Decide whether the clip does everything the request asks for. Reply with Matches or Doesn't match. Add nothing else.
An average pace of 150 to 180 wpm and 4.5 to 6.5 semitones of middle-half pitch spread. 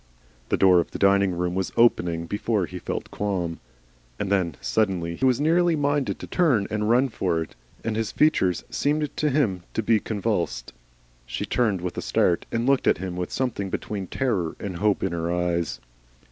Doesn't match